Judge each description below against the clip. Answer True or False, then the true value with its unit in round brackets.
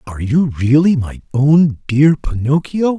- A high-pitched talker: False (145 Hz)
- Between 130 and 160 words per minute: True (140 wpm)